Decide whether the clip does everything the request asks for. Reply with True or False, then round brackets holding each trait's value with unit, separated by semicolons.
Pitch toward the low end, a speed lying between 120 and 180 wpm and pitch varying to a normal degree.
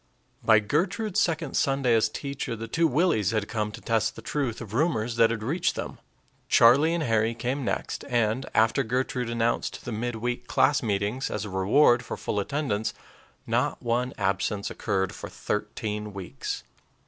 True (115 Hz; 170 wpm; 4.0 semitones)